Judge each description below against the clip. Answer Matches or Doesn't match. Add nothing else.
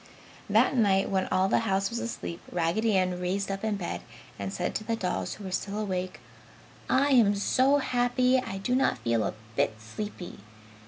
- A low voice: Doesn't match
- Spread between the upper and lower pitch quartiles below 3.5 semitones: Doesn't match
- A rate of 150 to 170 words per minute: Doesn't match